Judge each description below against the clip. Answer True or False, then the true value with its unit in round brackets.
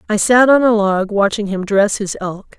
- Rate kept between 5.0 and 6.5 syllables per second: False (4.6 syllables/s)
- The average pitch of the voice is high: True (210 Hz)